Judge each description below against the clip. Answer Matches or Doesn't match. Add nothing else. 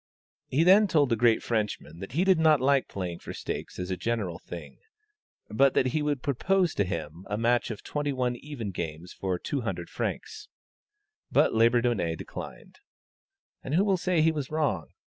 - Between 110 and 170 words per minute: Doesn't match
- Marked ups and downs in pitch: Matches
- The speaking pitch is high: Doesn't match